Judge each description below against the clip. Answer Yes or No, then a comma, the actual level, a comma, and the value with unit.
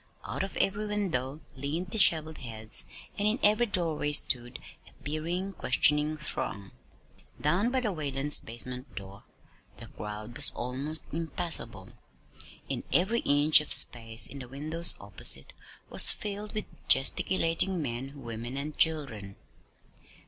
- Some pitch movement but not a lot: No, wide, 6.2 semitones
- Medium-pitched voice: Yes, medium, 150 Hz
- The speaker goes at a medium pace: No, slow, 130 wpm